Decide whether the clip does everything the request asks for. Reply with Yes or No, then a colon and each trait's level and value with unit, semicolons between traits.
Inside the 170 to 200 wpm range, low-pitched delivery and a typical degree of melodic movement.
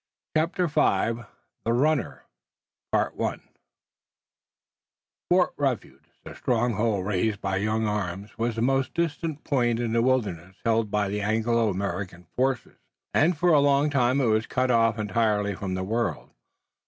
No: average, 140 wpm; low, 115 Hz; average, 4.4 semitones